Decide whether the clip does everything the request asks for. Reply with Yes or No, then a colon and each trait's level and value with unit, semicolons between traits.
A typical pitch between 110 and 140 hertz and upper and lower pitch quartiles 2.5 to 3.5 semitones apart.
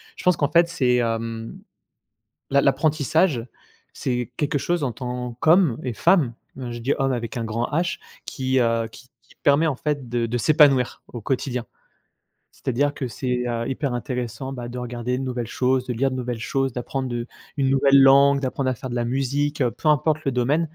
Yes: low, 130 Hz; average, 2.8 semitones